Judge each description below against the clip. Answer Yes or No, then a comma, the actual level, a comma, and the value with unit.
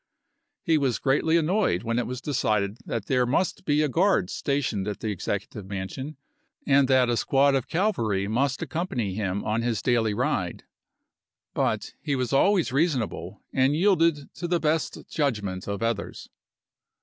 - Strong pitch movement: Yes, wide, 6.0 semitones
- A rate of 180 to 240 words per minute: No, average, 160 wpm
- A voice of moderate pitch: No, low, 130 Hz